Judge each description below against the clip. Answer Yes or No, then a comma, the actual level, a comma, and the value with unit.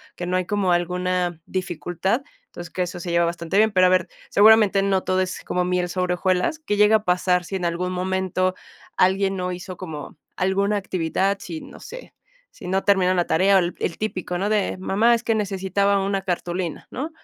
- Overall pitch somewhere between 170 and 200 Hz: Yes, medium, 185 Hz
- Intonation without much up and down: Yes, narrow, 1.8 semitones